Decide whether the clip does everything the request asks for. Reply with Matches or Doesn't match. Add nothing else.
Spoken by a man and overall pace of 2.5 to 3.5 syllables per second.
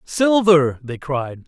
Matches